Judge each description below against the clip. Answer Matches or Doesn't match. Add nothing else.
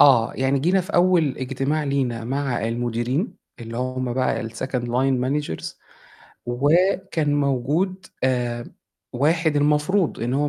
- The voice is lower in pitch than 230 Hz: Matches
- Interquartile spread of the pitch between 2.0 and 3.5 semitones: Doesn't match